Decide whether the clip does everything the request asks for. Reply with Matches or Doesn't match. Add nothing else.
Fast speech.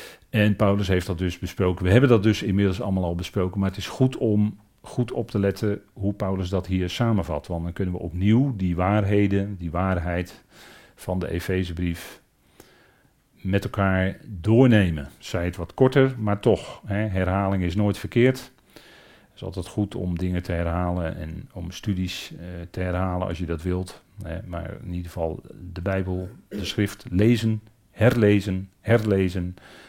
Doesn't match